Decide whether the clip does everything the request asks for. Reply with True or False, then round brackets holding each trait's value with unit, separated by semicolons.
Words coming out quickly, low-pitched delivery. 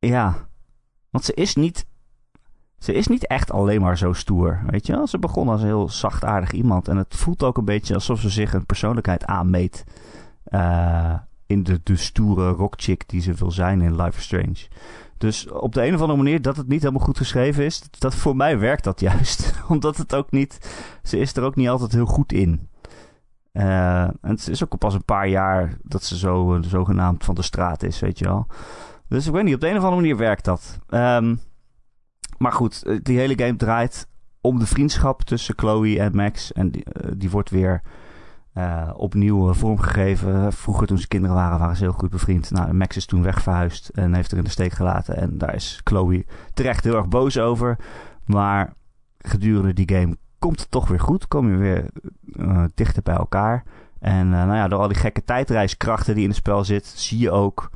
True (210 wpm; 100 Hz)